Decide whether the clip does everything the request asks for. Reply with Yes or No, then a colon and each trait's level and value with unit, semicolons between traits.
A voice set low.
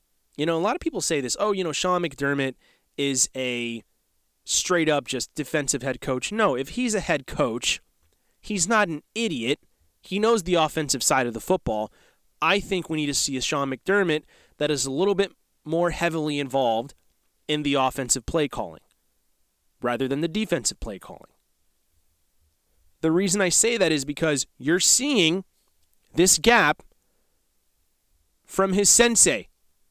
No: medium, 145 Hz